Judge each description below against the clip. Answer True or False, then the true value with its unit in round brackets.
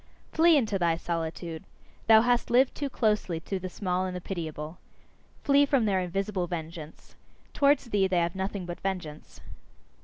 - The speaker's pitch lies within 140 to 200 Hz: True (185 Hz)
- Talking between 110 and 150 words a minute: False (160 wpm)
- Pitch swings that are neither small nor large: True (4.4 semitones)